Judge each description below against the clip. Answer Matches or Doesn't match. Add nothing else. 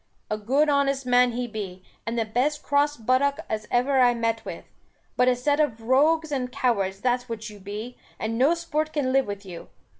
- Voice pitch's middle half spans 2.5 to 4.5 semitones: Matches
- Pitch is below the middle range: Doesn't match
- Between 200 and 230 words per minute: Matches